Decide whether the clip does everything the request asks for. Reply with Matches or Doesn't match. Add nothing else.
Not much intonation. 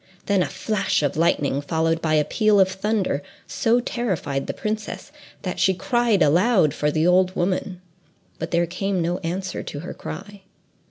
Doesn't match